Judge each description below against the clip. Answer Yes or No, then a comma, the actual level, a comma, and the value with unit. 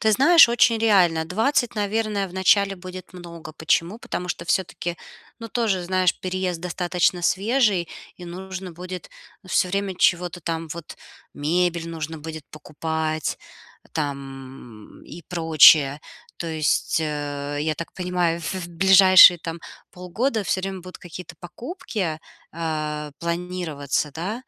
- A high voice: No, medium, 175 Hz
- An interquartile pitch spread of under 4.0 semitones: Yes, average, 2.9 semitones